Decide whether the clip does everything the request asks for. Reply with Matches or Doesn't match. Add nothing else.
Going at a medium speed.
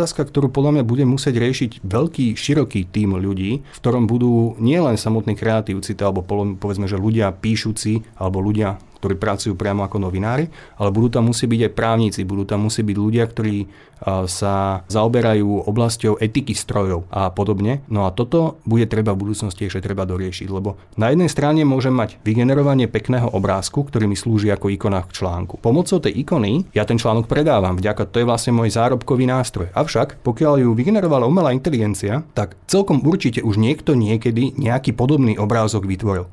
Doesn't match